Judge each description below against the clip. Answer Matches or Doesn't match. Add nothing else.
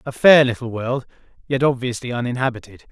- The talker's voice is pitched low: Matches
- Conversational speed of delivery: Matches